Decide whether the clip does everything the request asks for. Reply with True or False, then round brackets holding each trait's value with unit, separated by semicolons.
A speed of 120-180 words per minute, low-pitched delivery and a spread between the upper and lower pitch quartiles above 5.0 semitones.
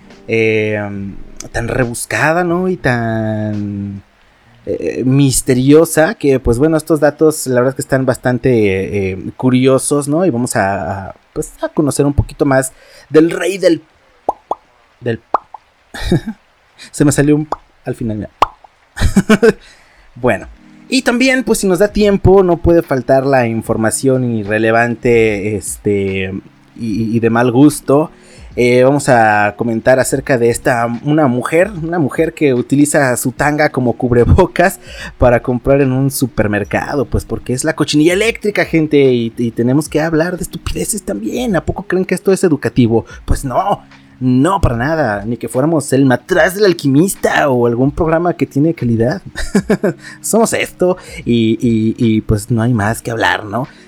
True (155 wpm; 130 Hz; 5.4 semitones)